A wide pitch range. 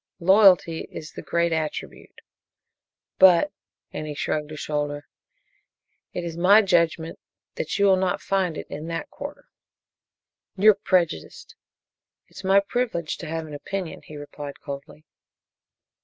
No: average, 3.8 semitones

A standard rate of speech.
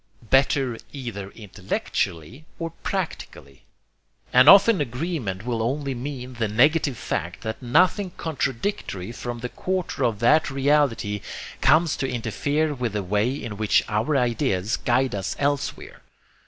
No: slow, 130 wpm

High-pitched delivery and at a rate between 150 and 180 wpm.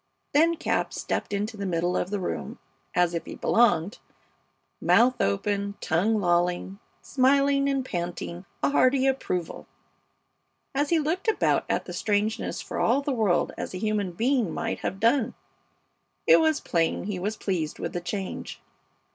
Yes: high, 205 Hz; average, 155 wpm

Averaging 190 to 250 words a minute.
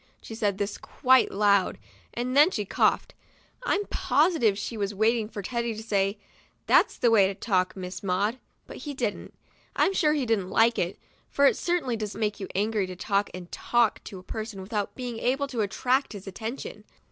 Yes: average, 200 wpm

